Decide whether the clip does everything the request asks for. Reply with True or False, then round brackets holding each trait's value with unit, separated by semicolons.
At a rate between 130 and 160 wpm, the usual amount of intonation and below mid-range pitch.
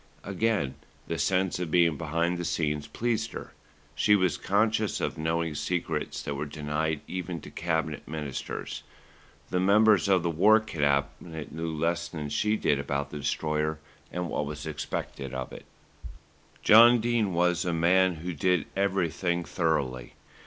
True (150 wpm; 3.6 semitones; 85 Hz)